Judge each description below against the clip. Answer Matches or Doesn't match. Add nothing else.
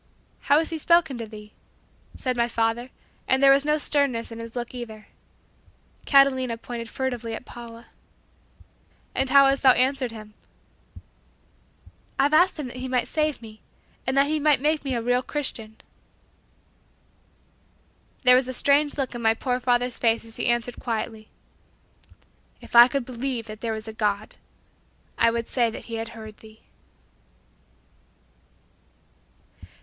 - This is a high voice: Matches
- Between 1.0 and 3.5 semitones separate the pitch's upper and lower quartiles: Matches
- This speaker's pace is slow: Doesn't match